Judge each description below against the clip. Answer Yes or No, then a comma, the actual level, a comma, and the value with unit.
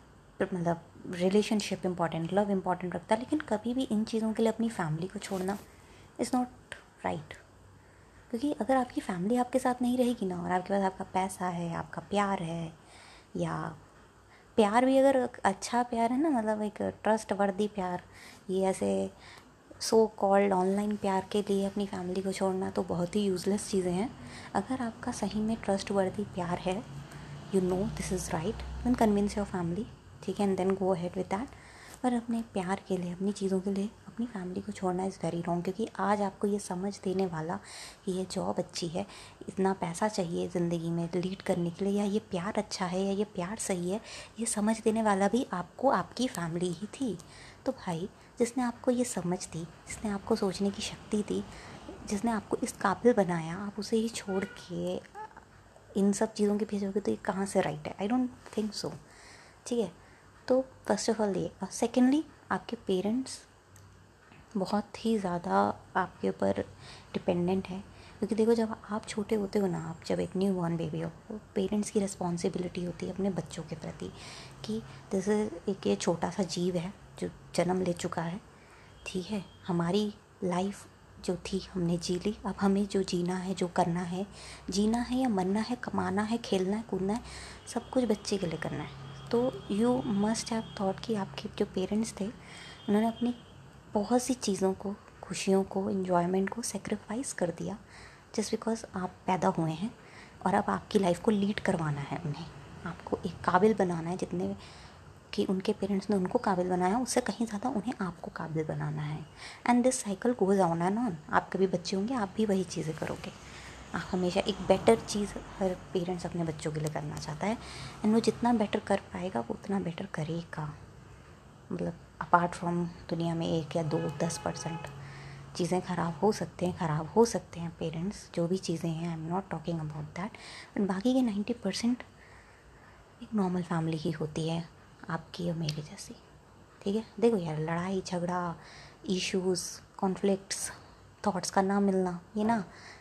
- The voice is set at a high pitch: Yes, high, 195 Hz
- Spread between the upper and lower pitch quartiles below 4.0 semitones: Yes, average, 3.3 semitones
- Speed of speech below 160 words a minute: No, average, 185 wpm